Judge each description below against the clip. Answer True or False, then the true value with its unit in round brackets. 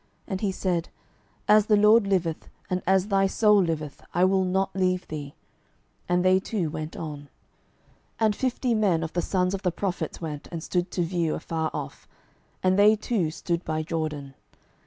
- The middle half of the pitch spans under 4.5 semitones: True (3.4 semitones)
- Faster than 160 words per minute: True (180 wpm)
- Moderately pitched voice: True (180 Hz)